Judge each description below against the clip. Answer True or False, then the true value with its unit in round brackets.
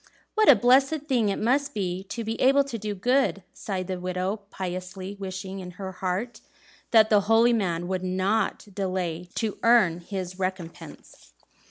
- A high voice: True (195 Hz)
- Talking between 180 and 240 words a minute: False (170 wpm)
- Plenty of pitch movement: False (3.8 semitones)